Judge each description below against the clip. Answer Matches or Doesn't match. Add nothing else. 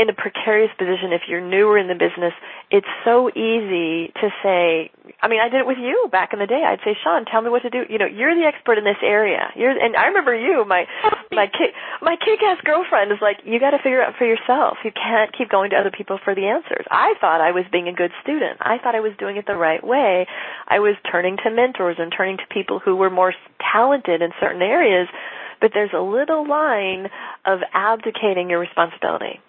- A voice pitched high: Matches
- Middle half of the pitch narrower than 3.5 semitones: Doesn't match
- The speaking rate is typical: Doesn't match